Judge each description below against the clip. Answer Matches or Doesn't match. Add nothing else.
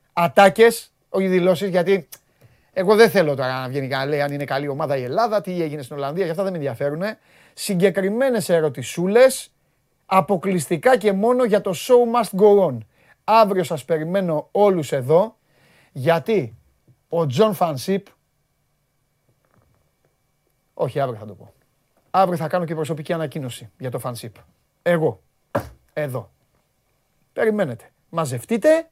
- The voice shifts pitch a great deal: Matches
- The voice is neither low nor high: Matches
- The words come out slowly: Doesn't match